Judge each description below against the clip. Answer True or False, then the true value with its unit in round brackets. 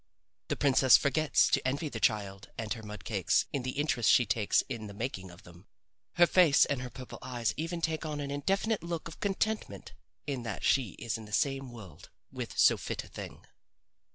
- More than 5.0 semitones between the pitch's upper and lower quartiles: True (5.6 semitones)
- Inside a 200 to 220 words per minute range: True (205 wpm)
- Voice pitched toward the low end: True (130 Hz)